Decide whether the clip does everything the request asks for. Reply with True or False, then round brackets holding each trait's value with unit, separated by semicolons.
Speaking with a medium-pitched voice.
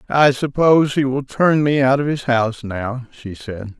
False (130 Hz)